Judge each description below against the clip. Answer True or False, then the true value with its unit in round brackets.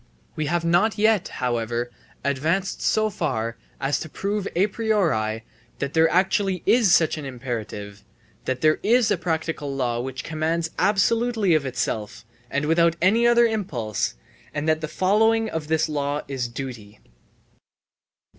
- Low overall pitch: False (160 Hz)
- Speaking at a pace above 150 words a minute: False (145 wpm)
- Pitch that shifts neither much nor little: False (7.0 semitones)